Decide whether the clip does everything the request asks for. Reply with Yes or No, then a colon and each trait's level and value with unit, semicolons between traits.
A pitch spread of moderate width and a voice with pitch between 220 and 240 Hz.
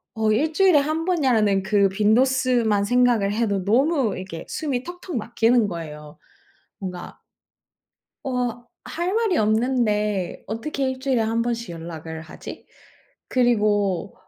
Yes: average, 4.6 semitones; high, 225 Hz